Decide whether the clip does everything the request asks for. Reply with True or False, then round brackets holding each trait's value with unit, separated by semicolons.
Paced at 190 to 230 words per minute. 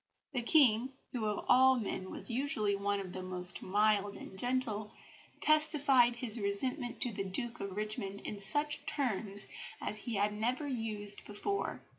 False (160 wpm)